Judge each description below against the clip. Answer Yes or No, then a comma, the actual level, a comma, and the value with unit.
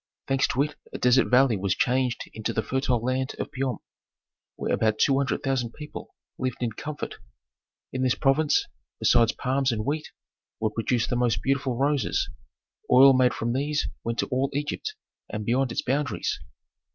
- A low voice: Yes, low, 130 Hz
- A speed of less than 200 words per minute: Yes, average, 170 wpm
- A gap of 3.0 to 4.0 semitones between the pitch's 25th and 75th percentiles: No, narrow, 2.6 semitones